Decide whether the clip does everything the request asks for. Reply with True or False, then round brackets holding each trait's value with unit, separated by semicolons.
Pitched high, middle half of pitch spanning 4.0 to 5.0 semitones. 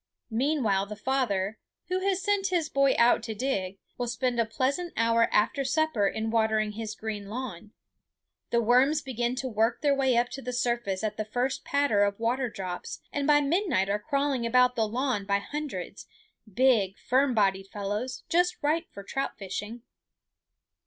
True (240 Hz; 4.6 semitones)